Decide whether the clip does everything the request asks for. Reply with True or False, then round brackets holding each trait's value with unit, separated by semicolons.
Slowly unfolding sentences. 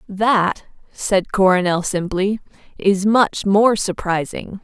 True (105 wpm)